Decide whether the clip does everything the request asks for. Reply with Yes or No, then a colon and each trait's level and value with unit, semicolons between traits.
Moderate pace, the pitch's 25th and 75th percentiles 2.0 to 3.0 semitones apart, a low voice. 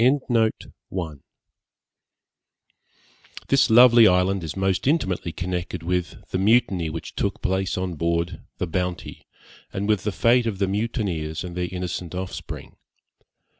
No: slow, 125 wpm; average, 2.7 semitones; very low, 95 Hz